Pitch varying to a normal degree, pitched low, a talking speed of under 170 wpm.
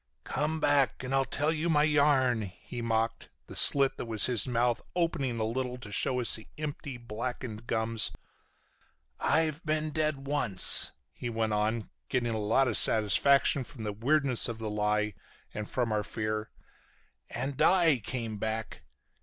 Yes: average, 4.3 semitones; low, 120 Hz; average, 160 wpm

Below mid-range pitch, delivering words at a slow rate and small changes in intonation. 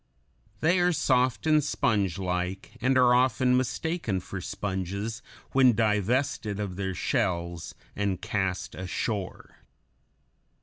No: low, 105 Hz; slow, 105 wpm; average, 5.2 semitones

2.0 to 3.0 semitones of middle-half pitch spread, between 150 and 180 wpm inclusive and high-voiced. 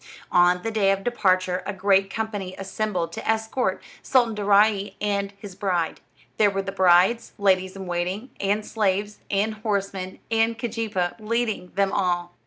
Yes: narrow, 2.6 semitones; average, 160 wpm; high, 200 Hz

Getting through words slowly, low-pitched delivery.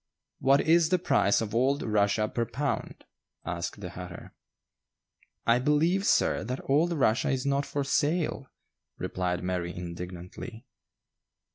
Yes: slow, 130 wpm; low, 125 Hz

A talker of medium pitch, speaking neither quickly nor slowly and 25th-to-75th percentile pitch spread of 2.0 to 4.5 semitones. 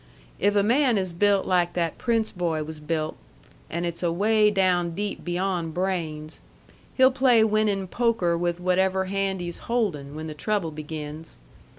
Yes: medium, 180 Hz; average, 160 wpm; average, 3.8 semitones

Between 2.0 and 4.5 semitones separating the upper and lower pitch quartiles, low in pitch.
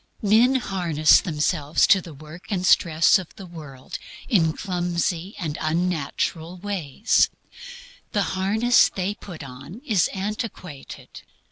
No: average, 4.2 semitones; medium, 180 Hz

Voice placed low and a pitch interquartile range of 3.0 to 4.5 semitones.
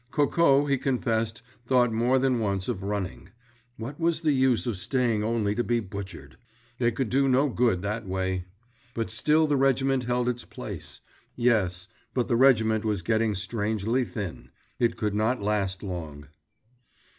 Yes: low, 115 Hz; average, 4.1 semitones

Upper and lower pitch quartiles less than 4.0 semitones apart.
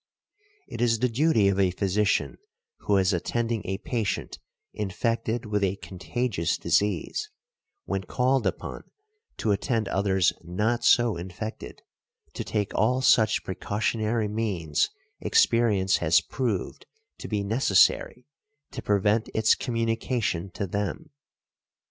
Yes: average, 3.2 semitones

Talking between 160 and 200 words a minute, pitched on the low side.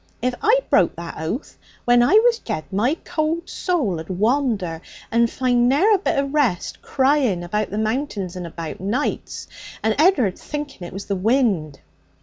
No: average, 170 wpm; high, 235 Hz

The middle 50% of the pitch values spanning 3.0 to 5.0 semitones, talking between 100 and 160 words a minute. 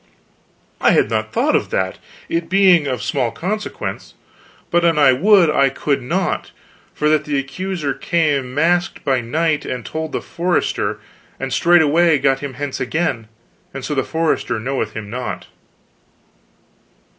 Yes: average, 4.4 semitones; average, 155 wpm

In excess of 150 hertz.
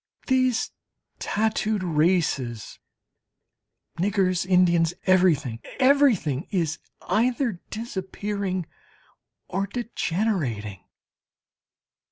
Yes: medium, 185 Hz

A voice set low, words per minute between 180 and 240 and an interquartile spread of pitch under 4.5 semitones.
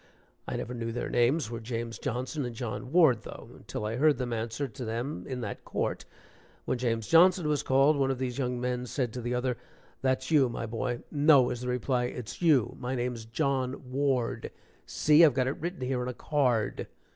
Yes: low, 125 Hz; fast, 205 wpm; narrow, 2.5 semitones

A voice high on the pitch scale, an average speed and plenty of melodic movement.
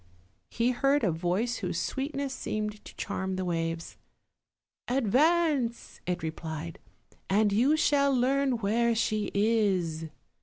No: high, 220 Hz; slow, 120 wpm; wide, 6.2 semitones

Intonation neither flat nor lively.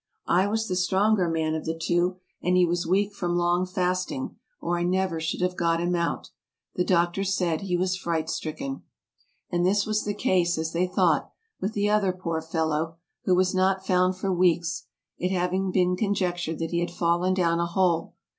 No: narrow, 1.7 semitones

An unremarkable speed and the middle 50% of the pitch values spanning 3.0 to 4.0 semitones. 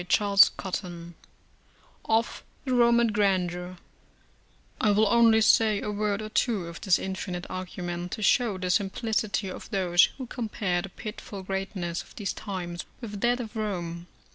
Yes: average, 150 wpm; average, 3.4 semitones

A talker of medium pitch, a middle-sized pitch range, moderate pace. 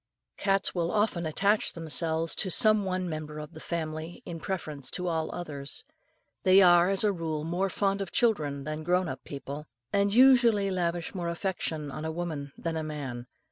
Yes: medium, 170 Hz; average, 3.7 semitones; average, 180 wpm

